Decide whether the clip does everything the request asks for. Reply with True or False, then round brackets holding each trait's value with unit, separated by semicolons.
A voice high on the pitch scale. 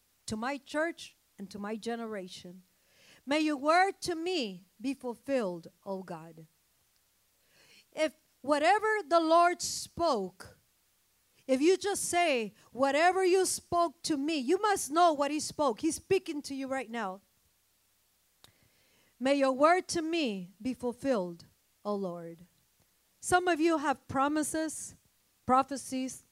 True (270 Hz)